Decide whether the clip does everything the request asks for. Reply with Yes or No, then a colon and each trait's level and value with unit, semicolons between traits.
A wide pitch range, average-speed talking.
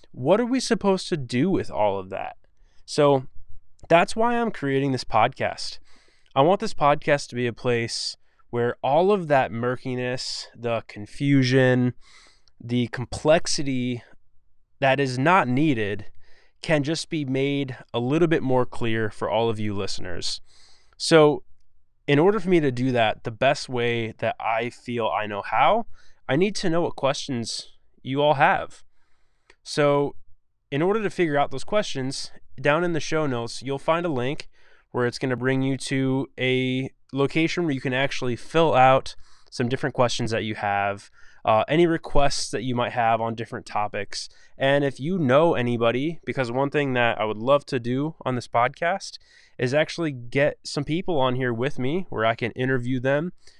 No: average, 4.0 semitones; average, 175 wpm